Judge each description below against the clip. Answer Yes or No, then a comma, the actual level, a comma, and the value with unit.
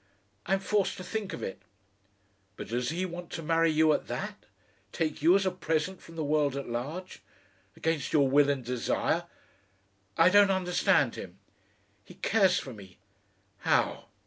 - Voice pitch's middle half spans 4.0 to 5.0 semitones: Yes, average, 4.5 semitones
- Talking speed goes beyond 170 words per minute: No, average, 165 wpm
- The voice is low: No, medium, 165 Hz